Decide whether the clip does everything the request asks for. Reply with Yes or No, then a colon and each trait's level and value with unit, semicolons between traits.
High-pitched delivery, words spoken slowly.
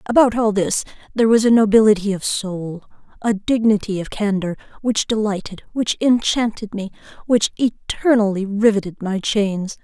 Yes: high, 210 Hz; slow, 115 wpm